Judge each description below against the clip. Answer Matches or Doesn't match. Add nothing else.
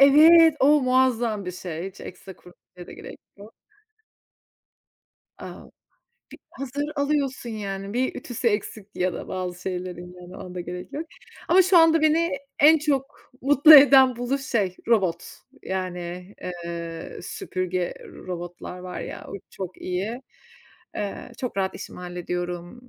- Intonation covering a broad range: Matches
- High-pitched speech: Matches